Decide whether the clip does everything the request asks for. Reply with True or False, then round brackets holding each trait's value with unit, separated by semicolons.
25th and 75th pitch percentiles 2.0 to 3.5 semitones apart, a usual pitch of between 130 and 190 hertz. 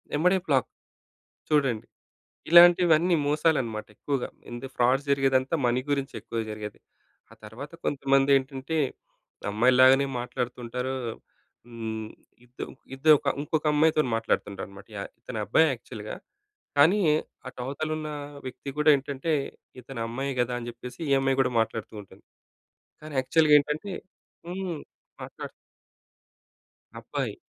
False (3.9 semitones; 135 Hz)